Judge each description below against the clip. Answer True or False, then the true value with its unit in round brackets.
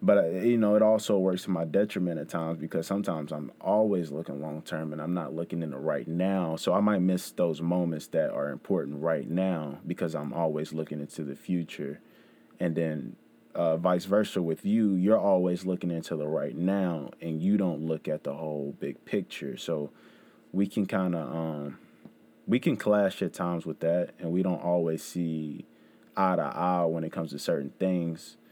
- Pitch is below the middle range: True (85 Hz)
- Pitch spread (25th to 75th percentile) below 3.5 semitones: True (2.7 semitones)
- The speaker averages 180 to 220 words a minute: True (200 wpm)